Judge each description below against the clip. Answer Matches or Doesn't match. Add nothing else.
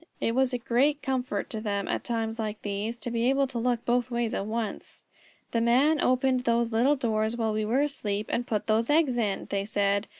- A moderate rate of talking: Doesn't match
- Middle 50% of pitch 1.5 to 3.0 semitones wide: Matches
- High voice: Matches